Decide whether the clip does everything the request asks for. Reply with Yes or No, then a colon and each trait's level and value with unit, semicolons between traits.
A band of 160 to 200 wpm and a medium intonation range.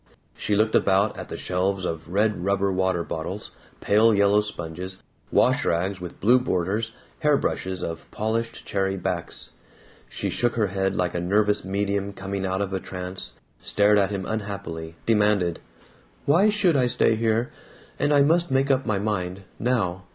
Yes: average, 165 wpm; average, 3.0 semitones